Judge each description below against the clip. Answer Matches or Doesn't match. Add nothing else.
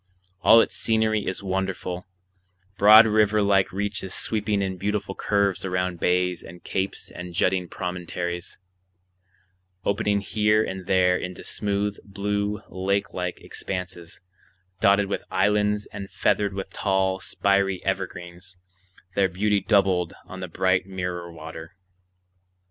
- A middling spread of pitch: Doesn't match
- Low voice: Matches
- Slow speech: Matches